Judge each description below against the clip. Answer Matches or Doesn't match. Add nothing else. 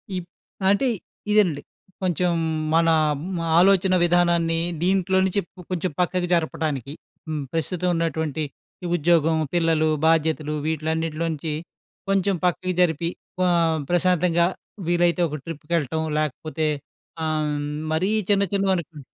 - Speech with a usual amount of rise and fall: Doesn't match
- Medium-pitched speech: Matches